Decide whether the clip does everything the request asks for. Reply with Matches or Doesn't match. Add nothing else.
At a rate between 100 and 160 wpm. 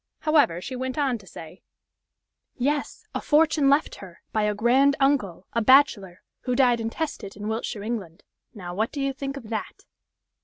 Doesn't match